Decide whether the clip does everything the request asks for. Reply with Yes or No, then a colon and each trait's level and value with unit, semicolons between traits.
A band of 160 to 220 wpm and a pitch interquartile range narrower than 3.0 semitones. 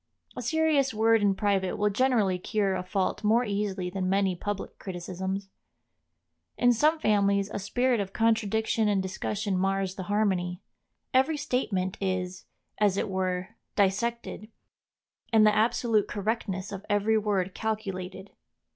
No: average, 140 wpm; narrow, 2.6 semitones